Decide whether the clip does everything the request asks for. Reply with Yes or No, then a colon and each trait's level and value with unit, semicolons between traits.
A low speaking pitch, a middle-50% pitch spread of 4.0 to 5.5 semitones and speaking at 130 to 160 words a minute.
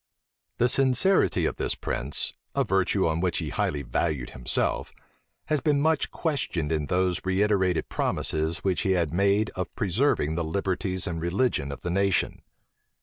Yes: very low, 95 Hz; average, 4.3 semitones; average, 155 wpm